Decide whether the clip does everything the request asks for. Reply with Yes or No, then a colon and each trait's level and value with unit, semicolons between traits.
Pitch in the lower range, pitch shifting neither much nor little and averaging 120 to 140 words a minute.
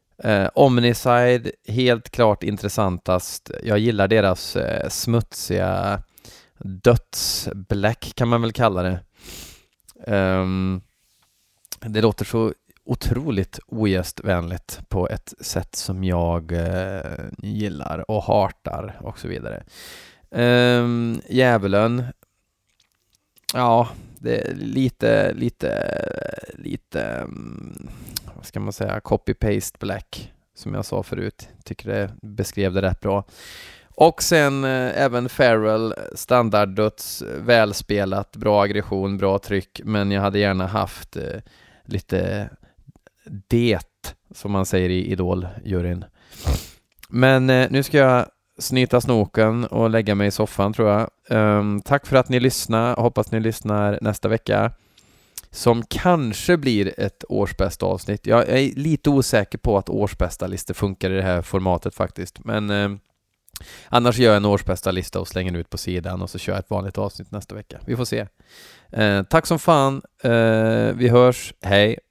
Yes: low, 105 Hz; average, 3.7 semitones; average, 130 wpm